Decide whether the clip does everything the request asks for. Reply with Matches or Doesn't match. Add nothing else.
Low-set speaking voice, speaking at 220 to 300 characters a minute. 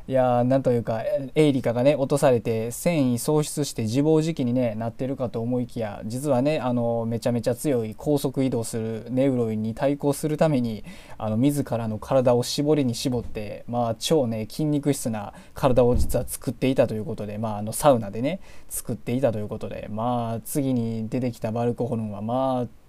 Doesn't match